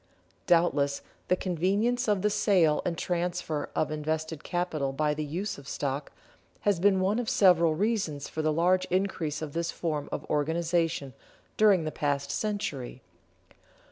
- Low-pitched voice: No, medium, 165 Hz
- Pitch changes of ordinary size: Yes, average, 3.8 semitones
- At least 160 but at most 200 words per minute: No, average, 150 wpm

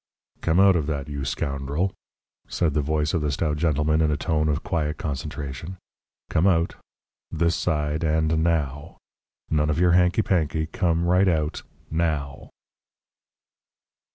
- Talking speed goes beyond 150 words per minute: No, average, 145 wpm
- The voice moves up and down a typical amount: No, narrow, 2.2 semitones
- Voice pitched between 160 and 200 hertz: No, very low, 80 Hz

